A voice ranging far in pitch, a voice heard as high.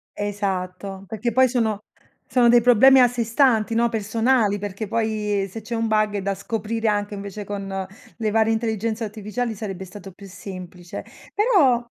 No: narrow, 2.5 semitones; high, 215 Hz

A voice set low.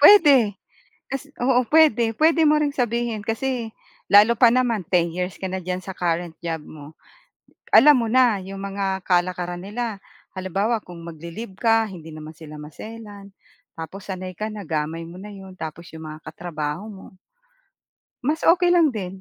No: high, 195 Hz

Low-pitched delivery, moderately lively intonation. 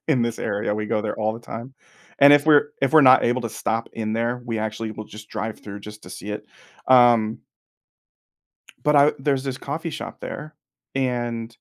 Yes: low, 115 Hz; average, 3.7 semitones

